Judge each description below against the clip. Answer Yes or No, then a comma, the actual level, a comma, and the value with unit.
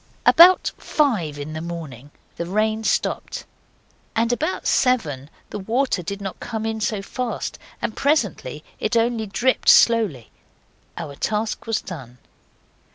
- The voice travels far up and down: Yes, wide, 6.2 semitones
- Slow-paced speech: Yes, slow, 130 wpm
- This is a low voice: No, high, 215 Hz